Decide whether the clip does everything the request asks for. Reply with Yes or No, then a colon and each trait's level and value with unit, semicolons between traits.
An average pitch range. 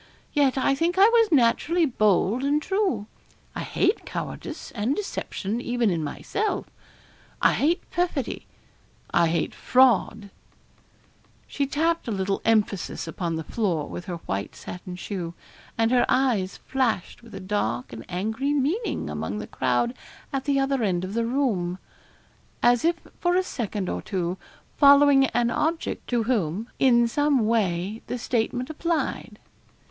No: wide, 6.9 semitones